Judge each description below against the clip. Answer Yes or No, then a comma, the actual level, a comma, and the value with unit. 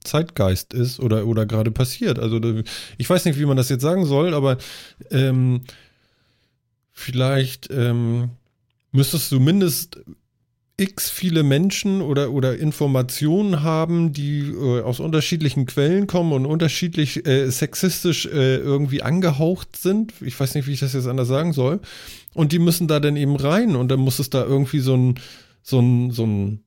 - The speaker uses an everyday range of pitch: Yes, average, 4.2 semitones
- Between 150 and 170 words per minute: Yes, average, 165 wpm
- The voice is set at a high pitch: No, low, 135 Hz